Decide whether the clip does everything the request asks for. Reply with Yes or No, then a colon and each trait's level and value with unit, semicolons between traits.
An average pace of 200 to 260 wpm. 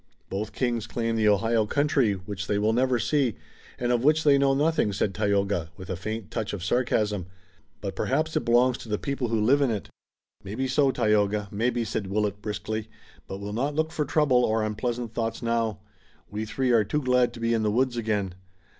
Yes: fast, 205 wpm